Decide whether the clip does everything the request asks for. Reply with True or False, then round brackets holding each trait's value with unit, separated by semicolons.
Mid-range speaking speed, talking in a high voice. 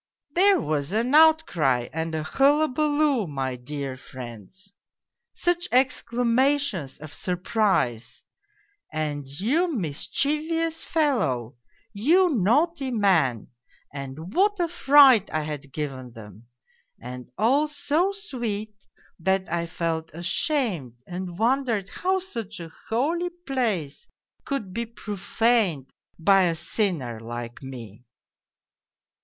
False (110 wpm; 200 Hz)